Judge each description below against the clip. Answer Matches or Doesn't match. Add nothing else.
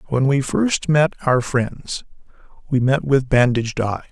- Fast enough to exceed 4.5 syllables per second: Doesn't match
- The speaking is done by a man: Matches